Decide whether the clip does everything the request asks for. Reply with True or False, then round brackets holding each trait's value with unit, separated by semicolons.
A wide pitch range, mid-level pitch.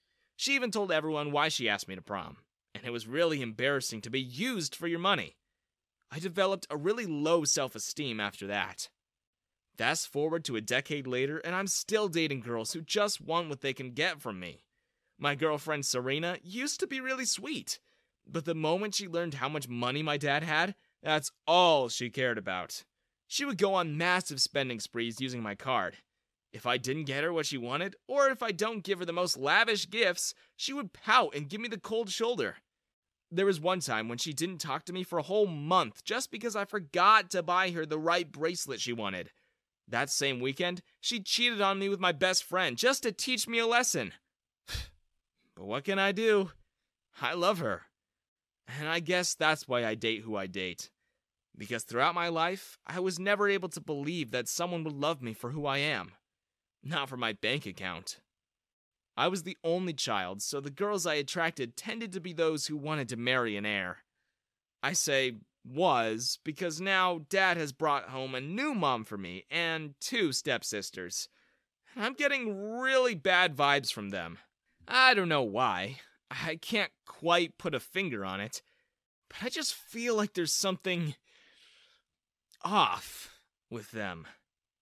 True (6.8 semitones; 165 Hz)